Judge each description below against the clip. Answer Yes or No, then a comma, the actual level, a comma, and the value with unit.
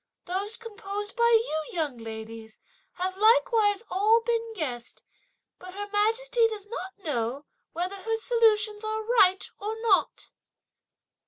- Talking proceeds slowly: Yes, slow, 130 wpm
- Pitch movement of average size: Yes, average, 3.8 semitones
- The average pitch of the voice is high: Yes, very high, 410 Hz